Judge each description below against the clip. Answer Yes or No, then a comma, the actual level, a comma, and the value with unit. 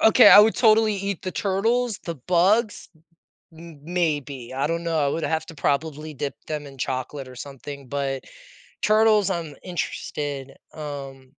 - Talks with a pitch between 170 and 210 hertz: No, medium, 155 Hz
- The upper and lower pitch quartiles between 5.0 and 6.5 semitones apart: Yes, wide, 5.6 semitones